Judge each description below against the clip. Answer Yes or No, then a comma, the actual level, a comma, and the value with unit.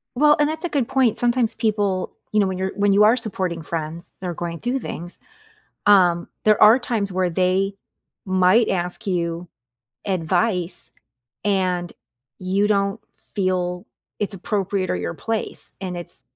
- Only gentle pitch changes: No, average, 3.2 semitones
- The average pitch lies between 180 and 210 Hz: Yes, high, 190 Hz